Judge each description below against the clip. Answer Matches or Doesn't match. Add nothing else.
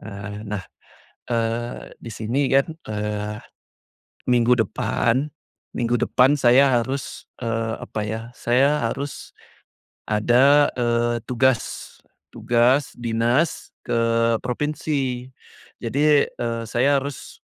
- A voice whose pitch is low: Matches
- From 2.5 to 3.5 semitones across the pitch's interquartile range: Matches